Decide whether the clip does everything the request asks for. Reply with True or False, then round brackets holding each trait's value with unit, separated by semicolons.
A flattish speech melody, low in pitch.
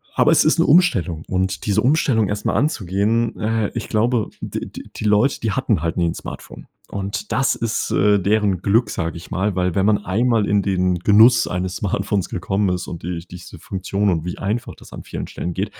False (3.2 semitones; 100 Hz)